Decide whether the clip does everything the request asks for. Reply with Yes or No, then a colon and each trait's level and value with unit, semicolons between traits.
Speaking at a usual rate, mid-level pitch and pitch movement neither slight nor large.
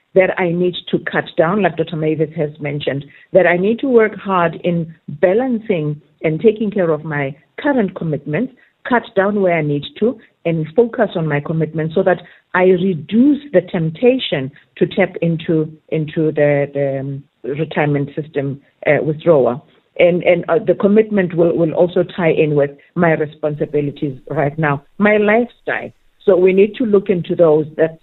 Yes: average, 165 wpm; medium, 170 Hz; average, 4.1 semitones